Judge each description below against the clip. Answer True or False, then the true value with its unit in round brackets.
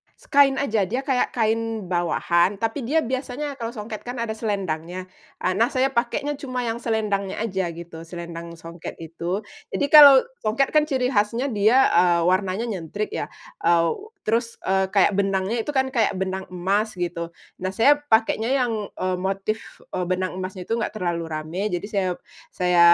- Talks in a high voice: True (205 Hz)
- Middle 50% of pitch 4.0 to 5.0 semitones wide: True (4.6 semitones)